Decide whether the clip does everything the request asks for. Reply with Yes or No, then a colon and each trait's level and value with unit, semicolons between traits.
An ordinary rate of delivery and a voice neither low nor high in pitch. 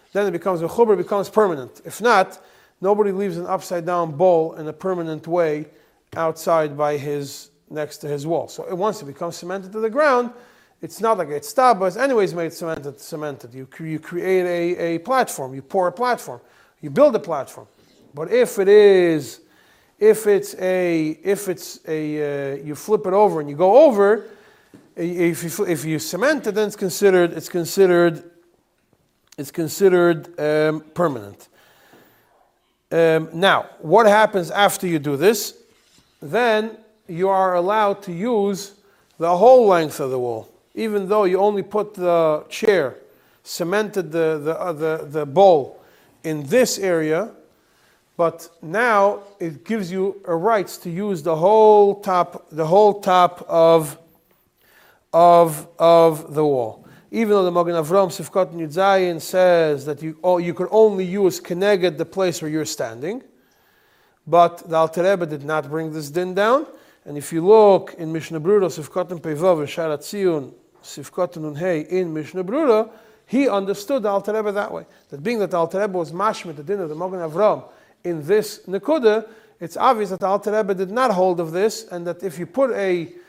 Yes: average, 165 wpm; medium, 180 Hz